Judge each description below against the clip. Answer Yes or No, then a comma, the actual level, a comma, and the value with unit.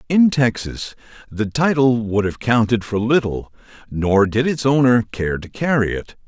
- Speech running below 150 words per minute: No, average, 165 wpm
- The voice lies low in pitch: Yes, low, 115 Hz